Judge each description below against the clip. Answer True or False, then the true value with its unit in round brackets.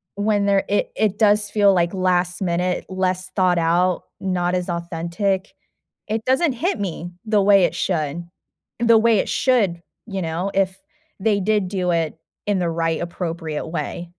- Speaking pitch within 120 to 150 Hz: False (185 Hz)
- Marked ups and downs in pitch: False (2.9 semitones)